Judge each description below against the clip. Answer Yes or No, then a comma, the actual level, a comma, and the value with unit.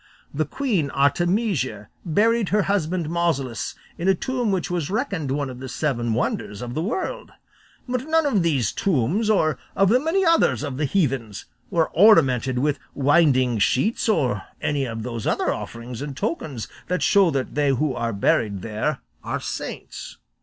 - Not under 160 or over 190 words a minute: Yes, average, 165 wpm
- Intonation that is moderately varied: No, wide, 7.6 semitones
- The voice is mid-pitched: Yes, medium, 150 Hz